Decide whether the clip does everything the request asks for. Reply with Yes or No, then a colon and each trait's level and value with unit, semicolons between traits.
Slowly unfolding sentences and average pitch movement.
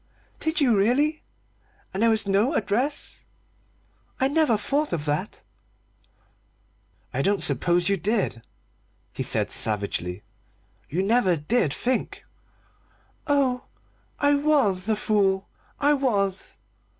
No: slow, 115 wpm; wide, 6.5 semitones